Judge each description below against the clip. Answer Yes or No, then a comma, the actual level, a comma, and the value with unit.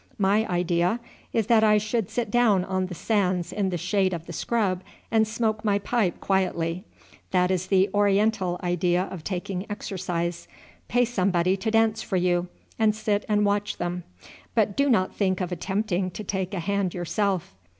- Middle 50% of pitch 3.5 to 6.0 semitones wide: No, average, 2.9 semitones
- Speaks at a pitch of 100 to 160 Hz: No, high, 195 Hz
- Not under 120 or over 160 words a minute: No, average, 175 wpm